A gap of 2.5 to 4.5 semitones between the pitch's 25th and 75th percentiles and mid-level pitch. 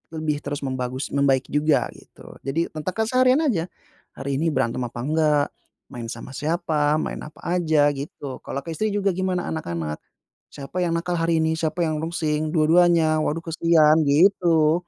Yes: average, 2.8 semitones; medium, 155 Hz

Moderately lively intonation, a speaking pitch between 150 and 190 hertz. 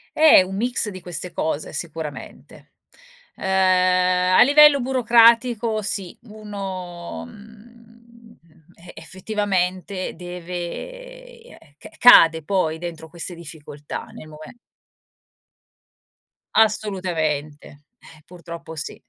Yes: average, 5.0 semitones; medium, 185 Hz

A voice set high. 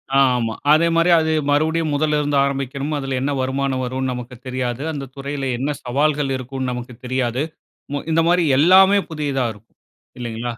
No: low, 135 Hz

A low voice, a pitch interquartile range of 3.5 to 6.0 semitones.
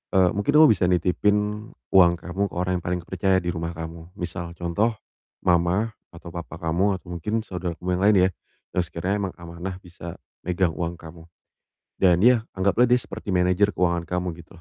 No: very low, 90 Hz; narrow, 2.4 semitones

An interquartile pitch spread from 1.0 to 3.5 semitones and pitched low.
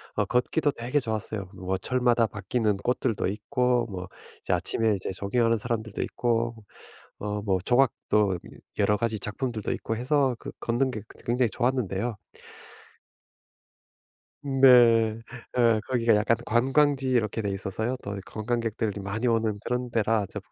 Yes: average, 2.9 semitones; low, 115 Hz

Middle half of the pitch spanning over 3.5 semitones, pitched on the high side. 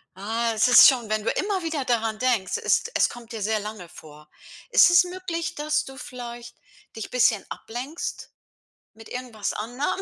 Yes: average, 5.2 semitones; high, 240 Hz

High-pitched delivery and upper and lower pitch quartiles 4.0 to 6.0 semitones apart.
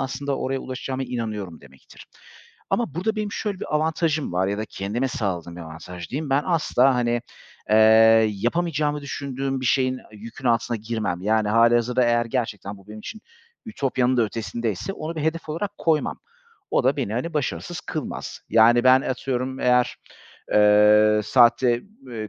No: low, 125 Hz; average, 4.7 semitones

